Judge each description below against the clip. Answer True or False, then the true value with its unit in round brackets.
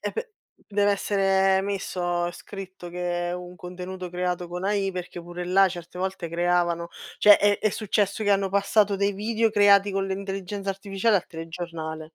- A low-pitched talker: False (190 Hz)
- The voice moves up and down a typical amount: False (2.1 semitones)